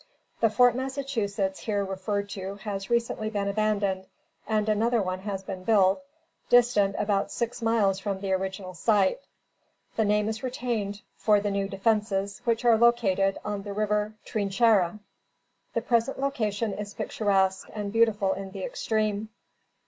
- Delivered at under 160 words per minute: Yes, average, 150 wpm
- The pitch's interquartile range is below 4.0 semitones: Yes, narrow, 2.4 semitones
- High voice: Yes, high, 210 Hz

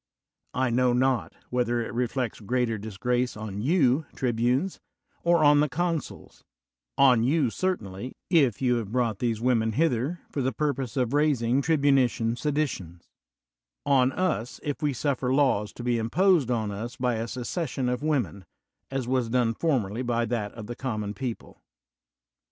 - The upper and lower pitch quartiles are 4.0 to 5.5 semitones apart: No, average, 3.5 semitones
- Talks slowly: No, average, 155 wpm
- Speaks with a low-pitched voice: Yes, low, 125 Hz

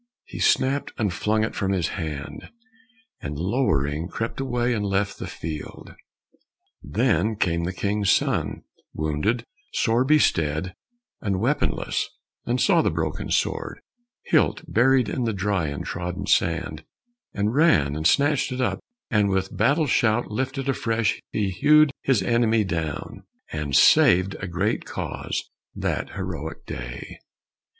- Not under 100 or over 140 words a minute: Yes, slow, 135 wpm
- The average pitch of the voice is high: No, low, 100 Hz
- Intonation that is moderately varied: No, wide, 6.4 semitones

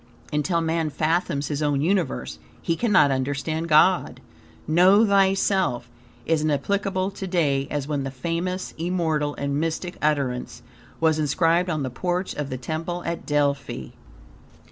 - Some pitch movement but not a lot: Yes, average, 3.9 semitones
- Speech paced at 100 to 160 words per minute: Yes, average, 145 wpm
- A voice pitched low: No, medium, 160 Hz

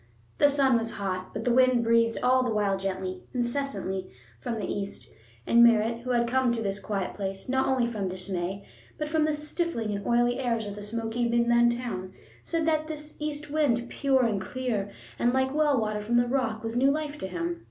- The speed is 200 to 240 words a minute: Yes, fast, 205 wpm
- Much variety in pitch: No, average, 4.3 semitones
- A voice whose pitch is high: Yes, high, 235 Hz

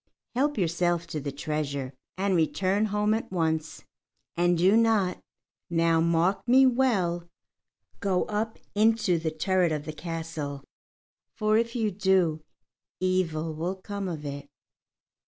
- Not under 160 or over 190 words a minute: No, slow, 135 wpm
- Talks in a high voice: No, medium, 180 Hz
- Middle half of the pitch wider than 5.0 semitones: No, average, 4.4 semitones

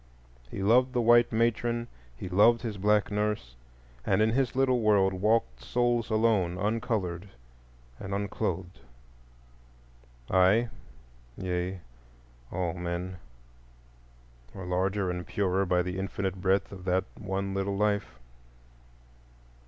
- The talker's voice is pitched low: Yes, very low, 95 Hz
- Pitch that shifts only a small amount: No, average, 3.4 semitones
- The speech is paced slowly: Yes, slow, 110 wpm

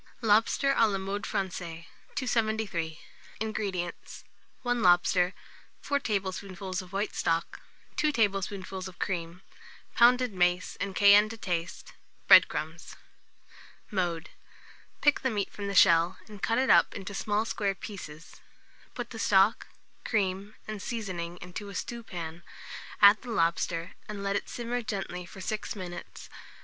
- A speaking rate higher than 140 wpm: No, slow, 135 wpm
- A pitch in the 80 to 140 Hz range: No, high, 195 Hz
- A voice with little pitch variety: No, average, 3.5 semitones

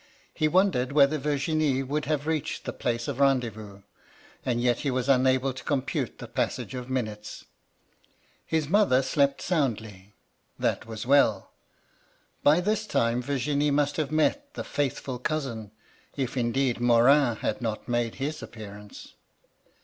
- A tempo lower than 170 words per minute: Yes, average, 150 wpm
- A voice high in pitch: No, low, 135 Hz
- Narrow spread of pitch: No, average, 3.7 semitones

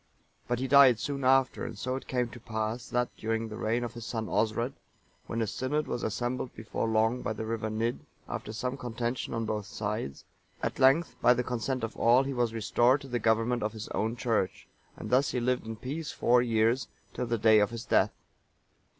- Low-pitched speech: Yes, low, 120 Hz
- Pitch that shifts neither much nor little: No, narrow, 2.3 semitones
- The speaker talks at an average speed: No, fast, 210 wpm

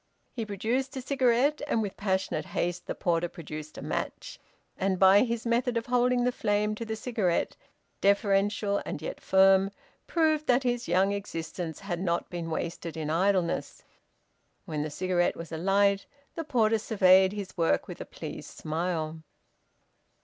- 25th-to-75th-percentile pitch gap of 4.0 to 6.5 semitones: Yes, average, 4.9 semitones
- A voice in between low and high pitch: No, high, 195 Hz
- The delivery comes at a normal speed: Yes, average, 155 wpm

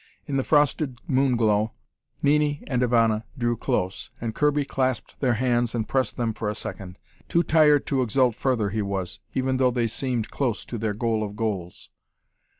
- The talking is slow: No, average, 180 wpm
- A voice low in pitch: Yes, low, 120 Hz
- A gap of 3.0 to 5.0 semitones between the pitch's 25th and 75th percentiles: Yes, average, 3.6 semitones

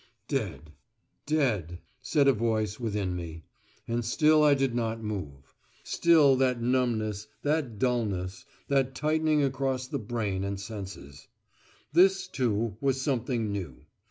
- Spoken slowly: Yes, slow, 130 wpm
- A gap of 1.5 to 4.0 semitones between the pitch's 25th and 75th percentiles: No, average, 5.0 semitones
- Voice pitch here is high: No, low, 120 Hz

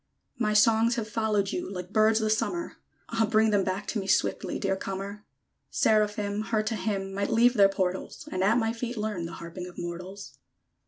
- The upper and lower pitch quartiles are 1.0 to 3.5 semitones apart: Yes, narrow, 2.4 semitones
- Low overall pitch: No, high, 210 Hz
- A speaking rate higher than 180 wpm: Yes, average, 195 wpm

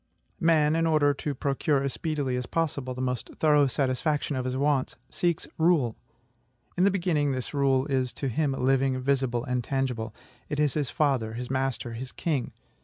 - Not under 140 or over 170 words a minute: No, average, 180 wpm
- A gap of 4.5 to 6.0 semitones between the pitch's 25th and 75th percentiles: No, average, 2.8 semitones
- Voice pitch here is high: No, low, 135 Hz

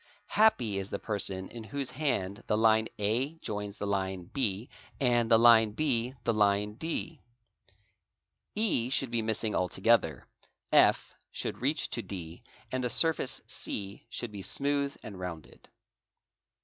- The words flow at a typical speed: Yes, average, 150 wpm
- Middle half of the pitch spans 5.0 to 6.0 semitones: No, average, 4.4 semitones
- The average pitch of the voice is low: Yes, low, 110 Hz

